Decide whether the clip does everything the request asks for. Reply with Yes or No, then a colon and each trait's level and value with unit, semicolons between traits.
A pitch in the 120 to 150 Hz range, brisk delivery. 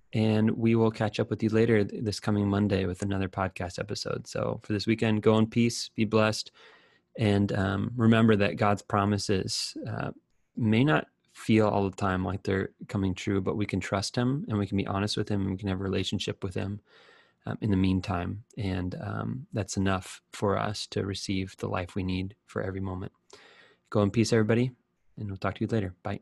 No: low, 105 Hz; fast, 210 wpm